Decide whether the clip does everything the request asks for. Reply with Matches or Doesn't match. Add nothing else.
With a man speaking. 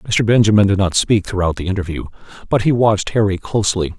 Matches